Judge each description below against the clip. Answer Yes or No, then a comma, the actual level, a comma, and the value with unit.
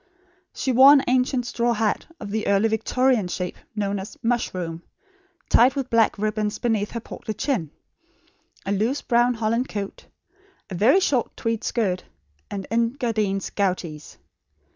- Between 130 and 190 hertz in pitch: No, high, 220 Hz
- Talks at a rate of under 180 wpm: Yes, average, 140 wpm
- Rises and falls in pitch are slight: No, average, 3.3 semitones